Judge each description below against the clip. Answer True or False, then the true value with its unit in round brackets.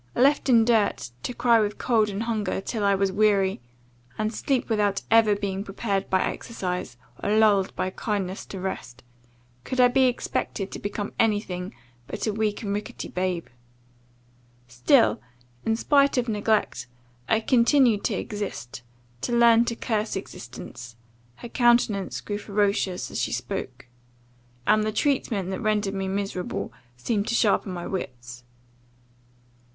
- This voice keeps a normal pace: True (150 wpm)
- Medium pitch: False (205 Hz)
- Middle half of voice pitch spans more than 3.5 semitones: False (3.1 semitones)